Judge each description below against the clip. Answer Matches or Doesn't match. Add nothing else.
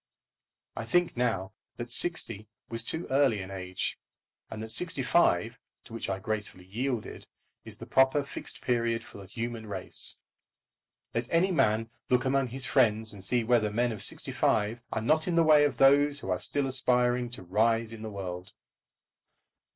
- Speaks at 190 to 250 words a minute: Doesn't match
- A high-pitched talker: Doesn't match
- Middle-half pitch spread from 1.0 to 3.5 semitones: Doesn't match